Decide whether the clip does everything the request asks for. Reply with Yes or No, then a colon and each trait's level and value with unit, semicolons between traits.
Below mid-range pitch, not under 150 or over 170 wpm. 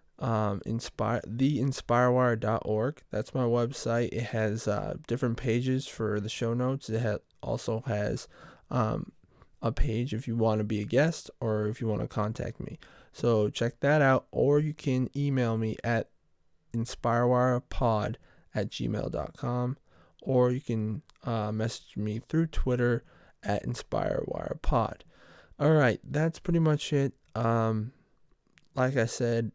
No: low, 120 Hz; average, 140 wpm